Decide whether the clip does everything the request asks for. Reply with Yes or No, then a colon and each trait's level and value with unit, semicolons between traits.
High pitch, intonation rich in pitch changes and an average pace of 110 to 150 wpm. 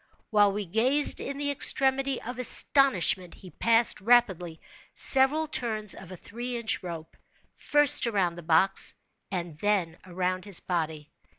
Yes: high, 205 Hz; wide, 6.0 semitones; average, 140 wpm